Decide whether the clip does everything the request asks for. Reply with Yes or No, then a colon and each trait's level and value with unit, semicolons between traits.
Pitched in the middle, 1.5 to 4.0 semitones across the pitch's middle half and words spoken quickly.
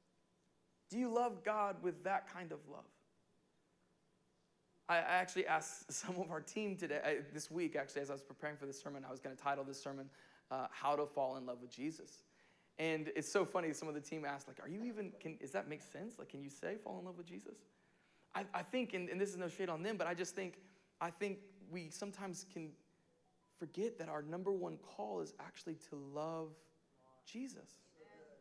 No: medium, 170 Hz; average, 4.5 semitones; fast, 215 wpm